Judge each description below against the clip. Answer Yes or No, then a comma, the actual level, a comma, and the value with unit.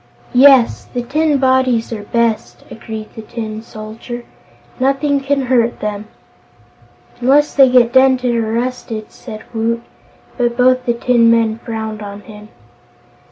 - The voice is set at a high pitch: Yes, high, 235 Hz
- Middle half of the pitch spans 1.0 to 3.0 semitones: Yes, average, 2.7 semitones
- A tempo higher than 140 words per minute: No, slow, 135 wpm